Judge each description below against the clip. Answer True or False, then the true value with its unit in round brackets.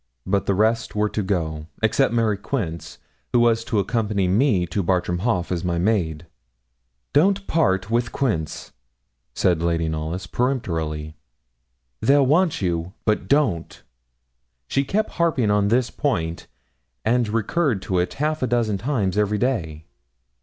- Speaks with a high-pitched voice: False (105 Hz)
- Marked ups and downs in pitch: True (6.0 semitones)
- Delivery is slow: False (145 wpm)